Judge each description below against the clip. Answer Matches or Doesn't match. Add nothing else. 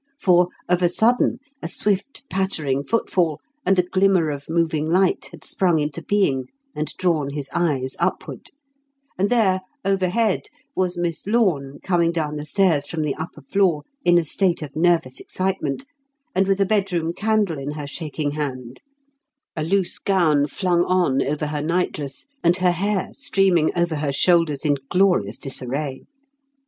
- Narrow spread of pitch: Doesn't match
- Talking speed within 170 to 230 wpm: Doesn't match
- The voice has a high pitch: Doesn't match